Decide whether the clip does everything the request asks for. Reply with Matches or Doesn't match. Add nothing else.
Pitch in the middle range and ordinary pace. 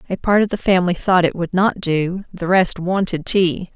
Doesn't match